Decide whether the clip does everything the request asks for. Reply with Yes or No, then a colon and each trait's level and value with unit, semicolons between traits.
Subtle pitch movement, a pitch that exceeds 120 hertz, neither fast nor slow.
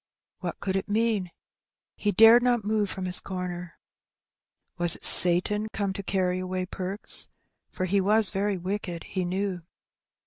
Yes: narrow, 2.3 semitones; high, 190 Hz; average, 150 wpm